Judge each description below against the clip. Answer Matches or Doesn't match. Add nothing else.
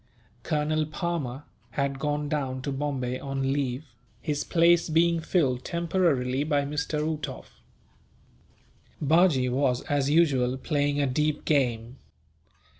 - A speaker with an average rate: Doesn't match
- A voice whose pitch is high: Doesn't match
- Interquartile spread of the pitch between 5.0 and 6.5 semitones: Doesn't match